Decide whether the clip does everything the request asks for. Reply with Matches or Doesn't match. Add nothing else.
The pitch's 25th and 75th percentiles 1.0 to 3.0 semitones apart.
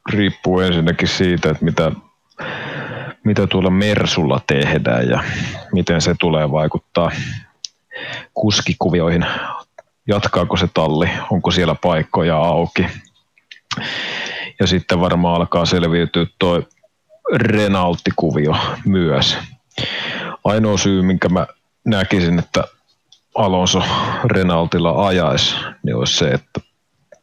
Matches